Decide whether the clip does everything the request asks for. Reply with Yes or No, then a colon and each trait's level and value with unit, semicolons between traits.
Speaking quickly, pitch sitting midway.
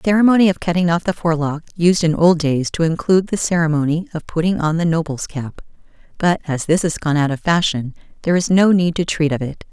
Yes: fast, 230 wpm; medium, 165 Hz